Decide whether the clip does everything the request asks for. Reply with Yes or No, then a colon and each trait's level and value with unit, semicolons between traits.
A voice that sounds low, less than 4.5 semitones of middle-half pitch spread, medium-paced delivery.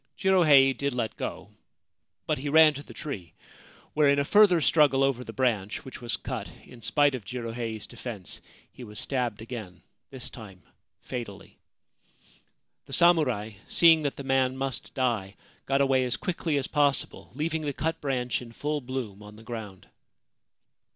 Yes: low, 130 Hz; average, 4.0 semitones; average, 165 wpm